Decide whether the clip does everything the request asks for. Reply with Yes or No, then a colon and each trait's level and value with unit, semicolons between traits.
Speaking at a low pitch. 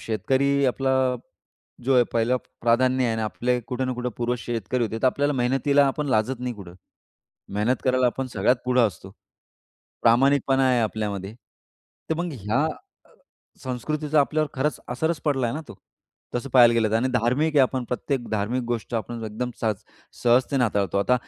Yes: low, 125 Hz